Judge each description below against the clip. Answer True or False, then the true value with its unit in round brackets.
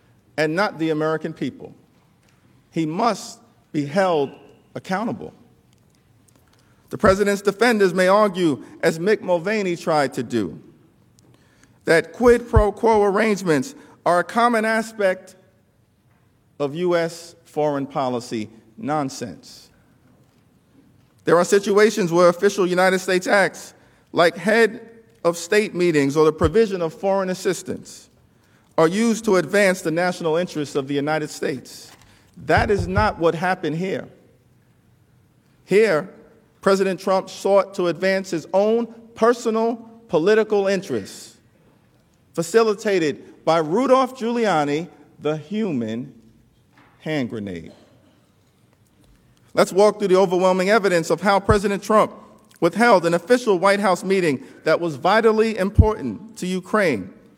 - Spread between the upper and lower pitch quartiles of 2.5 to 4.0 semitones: False (4.8 semitones)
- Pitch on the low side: False (185 Hz)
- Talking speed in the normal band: False (115 wpm)